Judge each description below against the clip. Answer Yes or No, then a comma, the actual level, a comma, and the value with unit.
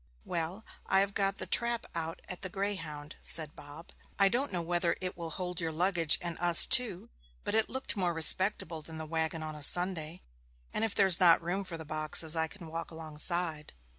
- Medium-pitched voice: Yes, medium, 170 Hz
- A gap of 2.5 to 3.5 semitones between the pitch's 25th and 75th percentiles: Yes, average, 3.1 semitones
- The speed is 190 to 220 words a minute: Yes, average, 200 wpm